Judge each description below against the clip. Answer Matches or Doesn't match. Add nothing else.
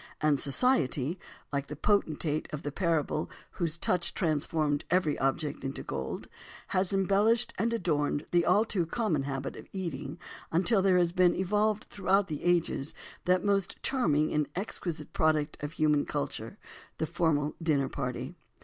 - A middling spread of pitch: Matches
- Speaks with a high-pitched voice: Doesn't match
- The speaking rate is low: Doesn't match